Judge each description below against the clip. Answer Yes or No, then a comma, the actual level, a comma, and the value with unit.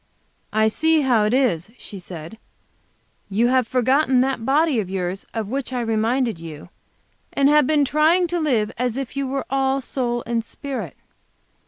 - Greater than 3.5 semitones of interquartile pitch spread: Yes, average, 4.0 semitones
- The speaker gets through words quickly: No, average, 170 wpm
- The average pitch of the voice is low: No, very high, 250 Hz